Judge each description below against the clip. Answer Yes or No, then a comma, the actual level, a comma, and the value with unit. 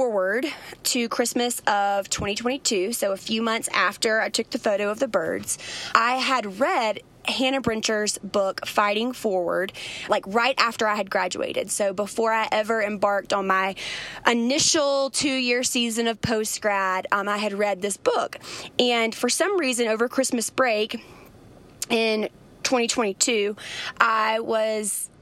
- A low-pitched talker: No, high, 225 Hz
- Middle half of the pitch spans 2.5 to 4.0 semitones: Yes, average, 3.3 semitones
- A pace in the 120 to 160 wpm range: Yes, average, 145 wpm